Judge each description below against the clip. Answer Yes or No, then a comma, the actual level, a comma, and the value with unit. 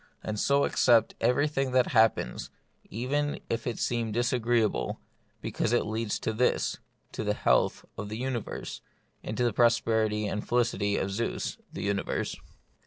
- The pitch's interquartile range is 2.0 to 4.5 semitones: Yes, narrow, 2.4 semitones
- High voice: No, low, 115 Hz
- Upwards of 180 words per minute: No, average, 160 wpm